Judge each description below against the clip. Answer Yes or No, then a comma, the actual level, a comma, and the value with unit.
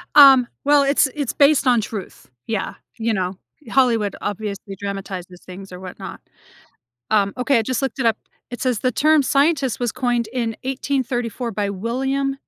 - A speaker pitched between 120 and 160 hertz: No, high, 240 Hz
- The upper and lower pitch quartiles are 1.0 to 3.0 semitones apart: No, average, 4.9 semitones